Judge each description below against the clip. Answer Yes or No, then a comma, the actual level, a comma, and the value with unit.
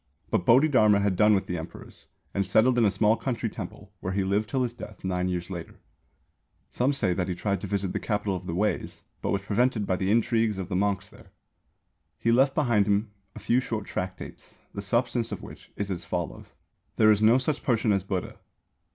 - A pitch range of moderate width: Yes, average, 3.5 semitones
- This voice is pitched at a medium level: No, low, 105 Hz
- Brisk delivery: Yes, fast, 210 wpm